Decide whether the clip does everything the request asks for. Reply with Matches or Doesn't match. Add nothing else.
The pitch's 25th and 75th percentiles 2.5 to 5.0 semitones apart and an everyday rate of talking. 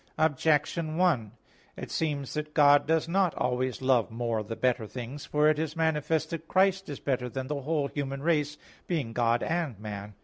Matches